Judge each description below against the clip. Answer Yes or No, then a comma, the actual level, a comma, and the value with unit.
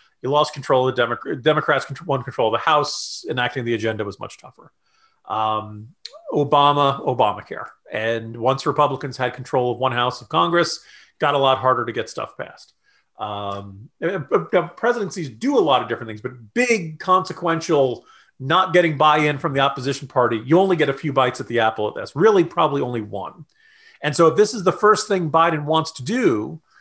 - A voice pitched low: No, medium, 145 Hz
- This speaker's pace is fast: No, average, 190 wpm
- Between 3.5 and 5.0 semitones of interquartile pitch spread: No, wide, 5.4 semitones